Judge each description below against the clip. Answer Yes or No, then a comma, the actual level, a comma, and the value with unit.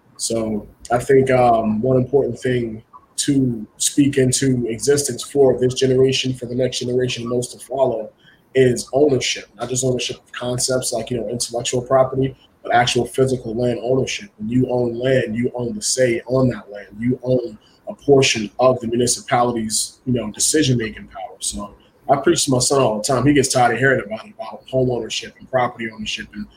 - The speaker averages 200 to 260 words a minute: No, average, 185 wpm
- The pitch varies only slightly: Yes, narrow, 2.2 semitones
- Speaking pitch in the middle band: No, low, 125 Hz